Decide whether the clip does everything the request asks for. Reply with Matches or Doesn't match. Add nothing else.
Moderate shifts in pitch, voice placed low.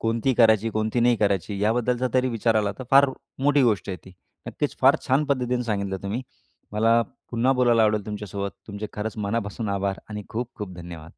Matches